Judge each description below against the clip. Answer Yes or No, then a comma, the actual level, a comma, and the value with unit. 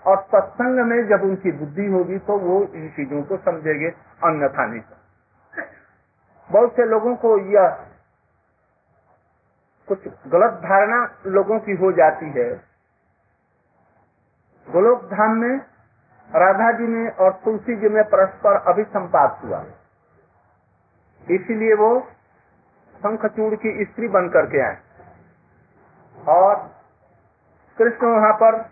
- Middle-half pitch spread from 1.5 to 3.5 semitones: No, average, 5.0 semitones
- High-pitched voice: Yes, high, 205 Hz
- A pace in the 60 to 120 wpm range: Yes, average, 115 wpm